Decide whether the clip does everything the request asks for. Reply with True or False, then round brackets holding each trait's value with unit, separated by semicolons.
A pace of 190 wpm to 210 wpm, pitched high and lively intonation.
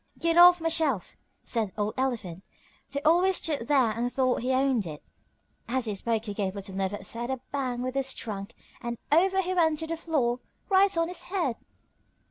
True (200 wpm; 260 Hz; 6.6 semitones)